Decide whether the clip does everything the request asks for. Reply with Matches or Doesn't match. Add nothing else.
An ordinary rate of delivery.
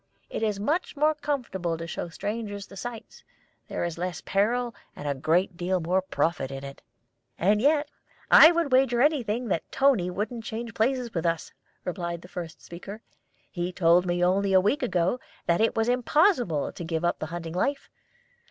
Matches